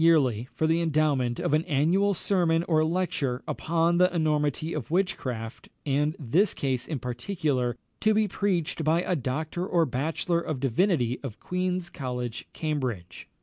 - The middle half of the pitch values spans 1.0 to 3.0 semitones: No, average, 5.1 semitones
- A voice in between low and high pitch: Yes, medium, 155 Hz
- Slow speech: No, average, 150 wpm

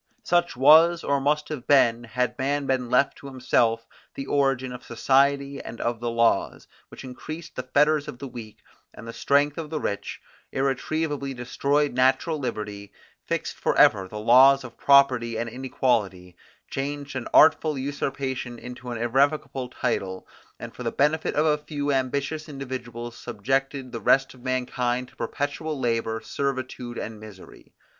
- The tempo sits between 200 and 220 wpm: No, average, 160 wpm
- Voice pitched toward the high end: No, low, 130 Hz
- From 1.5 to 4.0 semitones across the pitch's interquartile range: Yes, average, 3.0 semitones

